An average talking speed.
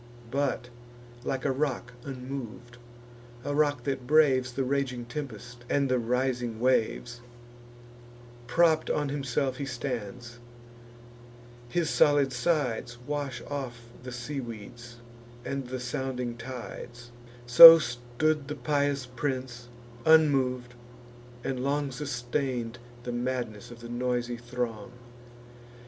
No: slow, 110 wpm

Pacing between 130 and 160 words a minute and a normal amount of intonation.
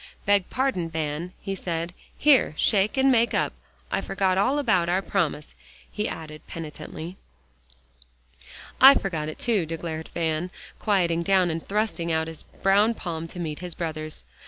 Yes: average, 155 wpm; average, 3.9 semitones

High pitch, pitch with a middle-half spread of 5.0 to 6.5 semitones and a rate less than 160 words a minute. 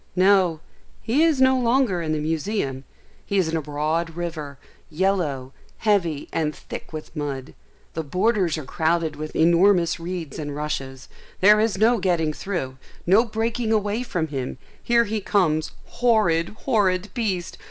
No: medium, 175 Hz; wide, 5.4 semitones; average, 150 wpm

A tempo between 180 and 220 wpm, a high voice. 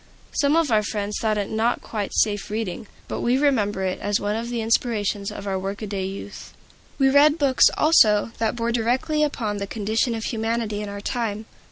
Yes: average, 195 wpm; high, 220 Hz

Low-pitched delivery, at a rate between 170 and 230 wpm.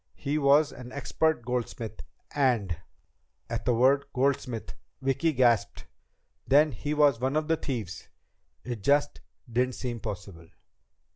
No: low, 130 Hz; slow, 135 wpm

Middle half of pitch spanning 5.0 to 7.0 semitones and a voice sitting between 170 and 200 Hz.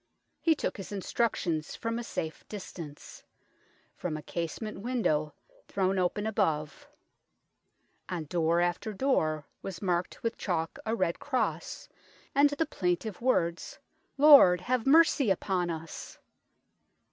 Yes: wide, 5.6 semitones; medium, 185 Hz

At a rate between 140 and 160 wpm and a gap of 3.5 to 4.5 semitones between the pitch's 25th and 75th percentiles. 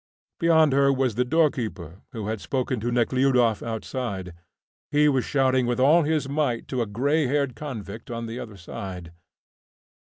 Yes: average, 155 wpm; average, 3.8 semitones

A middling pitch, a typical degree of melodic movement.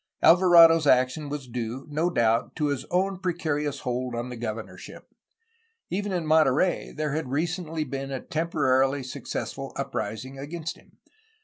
Yes: medium, 145 Hz; average, 4.3 semitones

